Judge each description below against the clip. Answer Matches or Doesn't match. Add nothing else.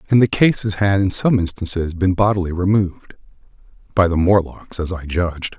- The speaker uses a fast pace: Doesn't match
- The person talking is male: Matches